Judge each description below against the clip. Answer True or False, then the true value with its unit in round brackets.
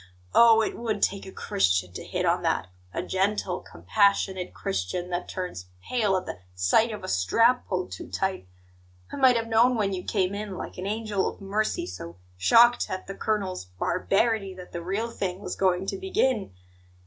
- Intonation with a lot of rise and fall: False (3.6 semitones)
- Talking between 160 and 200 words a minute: True (185 wpm)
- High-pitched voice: True (195 Hz)